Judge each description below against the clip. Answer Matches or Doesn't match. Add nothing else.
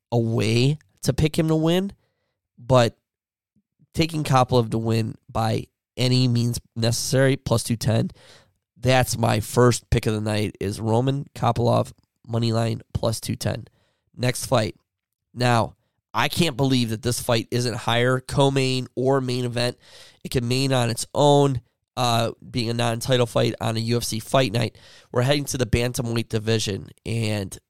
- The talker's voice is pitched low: Matches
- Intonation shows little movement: Matches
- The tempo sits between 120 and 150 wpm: Doesn't match